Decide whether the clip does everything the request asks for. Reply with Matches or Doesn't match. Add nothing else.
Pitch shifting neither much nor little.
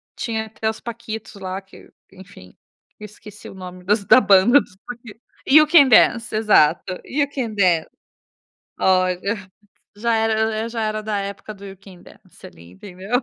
Matches